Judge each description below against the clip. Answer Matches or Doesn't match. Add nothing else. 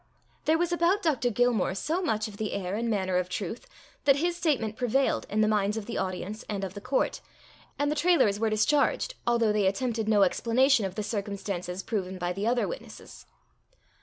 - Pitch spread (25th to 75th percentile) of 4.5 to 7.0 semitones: Matches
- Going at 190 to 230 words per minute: Matches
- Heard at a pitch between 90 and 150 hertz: Doesn't match